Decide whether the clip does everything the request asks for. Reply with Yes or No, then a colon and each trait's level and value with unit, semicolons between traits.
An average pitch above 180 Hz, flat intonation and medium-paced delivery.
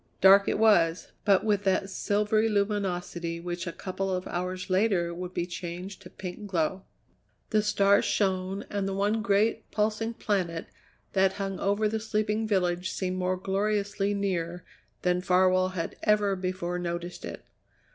Yes: high, 190 Hz; narrow, 2.3 semitones; average, 155 wpm